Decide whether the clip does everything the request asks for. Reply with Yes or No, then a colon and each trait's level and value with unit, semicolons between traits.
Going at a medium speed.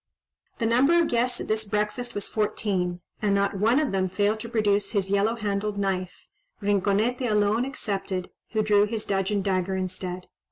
Yes: average, 170 wpm